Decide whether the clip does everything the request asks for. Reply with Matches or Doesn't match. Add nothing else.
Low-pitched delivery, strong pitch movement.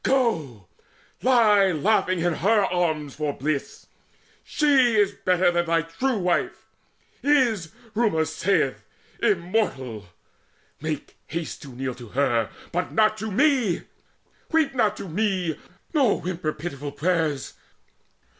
Doesn't match